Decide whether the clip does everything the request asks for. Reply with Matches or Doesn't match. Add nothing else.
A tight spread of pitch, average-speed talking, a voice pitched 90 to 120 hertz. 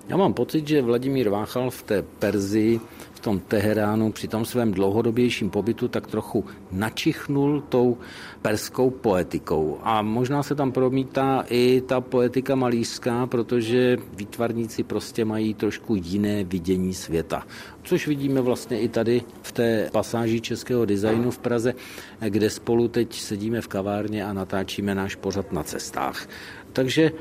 Doesn't match